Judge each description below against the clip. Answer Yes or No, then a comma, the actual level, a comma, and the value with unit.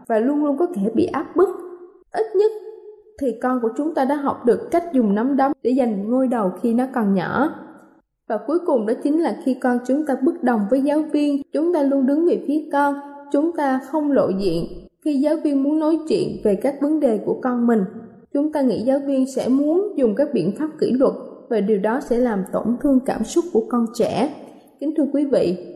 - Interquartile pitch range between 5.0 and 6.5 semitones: No, average, 4.0 semitones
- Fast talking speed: No, average, 230 wpm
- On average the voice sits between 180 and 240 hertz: No, very high, 275 Hz